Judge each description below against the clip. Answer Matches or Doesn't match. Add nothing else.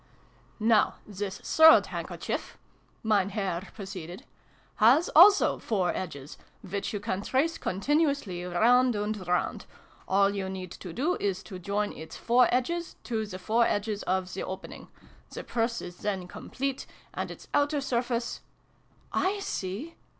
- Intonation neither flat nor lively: Matches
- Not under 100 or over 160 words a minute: Matches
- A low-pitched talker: Doesn't match